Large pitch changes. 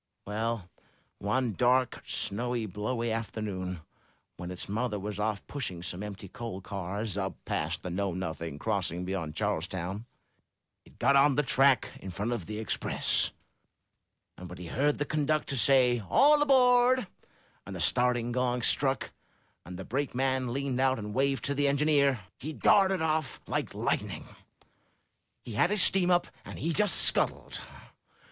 Yes: wide, 6.1 semitones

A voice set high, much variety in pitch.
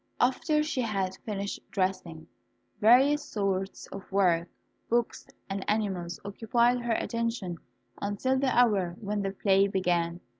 No: high, 200 Hz; average, 3.9 semitones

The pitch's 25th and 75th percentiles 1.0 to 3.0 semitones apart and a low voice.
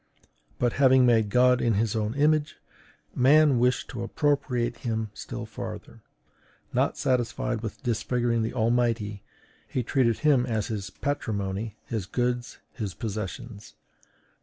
Yes: narrow, 2.4 semitones; low, 120 Hz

